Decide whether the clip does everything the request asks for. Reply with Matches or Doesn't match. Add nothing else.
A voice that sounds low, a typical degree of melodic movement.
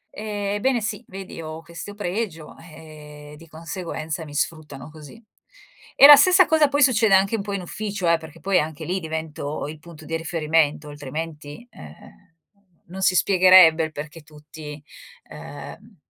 Doesn't match